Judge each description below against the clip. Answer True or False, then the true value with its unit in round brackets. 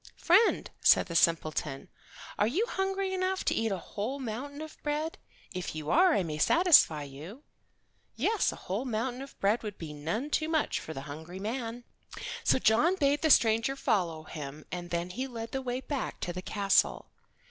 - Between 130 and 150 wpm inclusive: False (185 wpm)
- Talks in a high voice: True (225 Hz)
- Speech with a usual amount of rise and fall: False (8.9 semitones)